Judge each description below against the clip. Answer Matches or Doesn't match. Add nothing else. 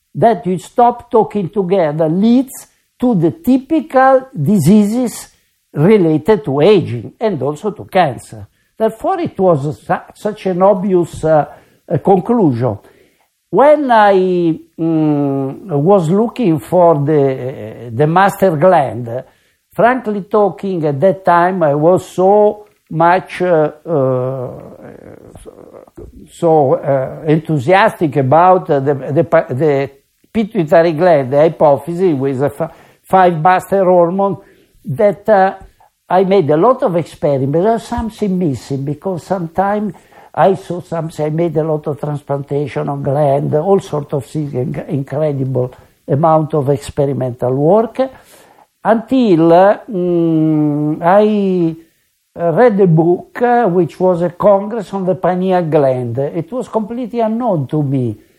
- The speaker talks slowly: Matches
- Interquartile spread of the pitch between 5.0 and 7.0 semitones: Matches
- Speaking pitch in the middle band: Matches